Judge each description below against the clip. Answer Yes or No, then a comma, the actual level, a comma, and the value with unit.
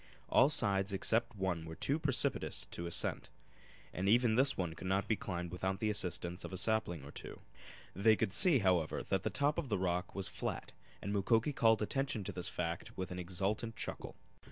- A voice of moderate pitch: No, very low, 95 Hz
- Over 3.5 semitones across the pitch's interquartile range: Yes, average, 3.9 semitones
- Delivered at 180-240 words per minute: Yes, average, 200 wpm